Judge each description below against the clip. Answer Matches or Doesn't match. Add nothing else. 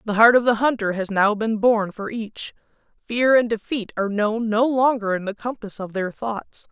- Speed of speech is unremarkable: Doesn't match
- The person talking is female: Matches